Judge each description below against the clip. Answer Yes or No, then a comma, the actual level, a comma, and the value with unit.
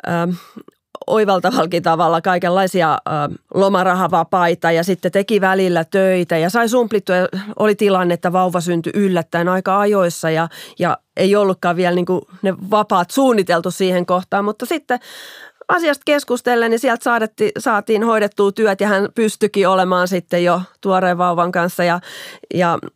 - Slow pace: No, average, 140 wpm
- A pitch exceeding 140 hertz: Yes, high, 190 Hz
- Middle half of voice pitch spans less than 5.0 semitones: Yes, average, 3.0 semitones